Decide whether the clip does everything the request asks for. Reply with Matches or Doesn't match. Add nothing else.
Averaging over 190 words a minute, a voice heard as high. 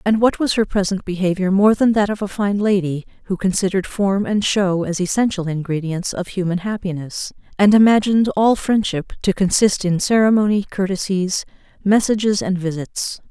Doesn't match